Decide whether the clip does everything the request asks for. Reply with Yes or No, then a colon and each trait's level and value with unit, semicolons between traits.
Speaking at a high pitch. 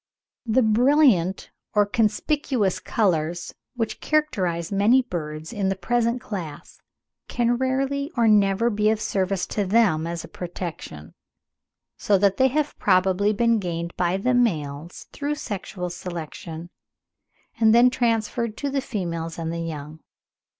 Yes: high, 205 Hz